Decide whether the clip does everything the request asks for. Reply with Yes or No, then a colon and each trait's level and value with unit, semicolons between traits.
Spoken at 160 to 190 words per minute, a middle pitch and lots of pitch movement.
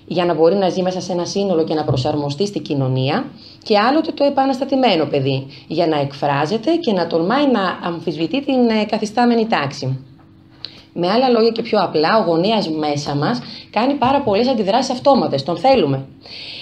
Yes: fast, 170 wpm; medium, 180 Hz; wide, 7.9 semitones